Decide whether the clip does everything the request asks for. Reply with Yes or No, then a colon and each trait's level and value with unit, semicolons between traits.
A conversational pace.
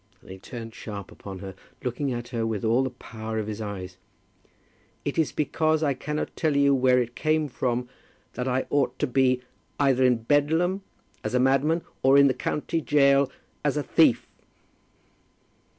Yes: average, 175 wpm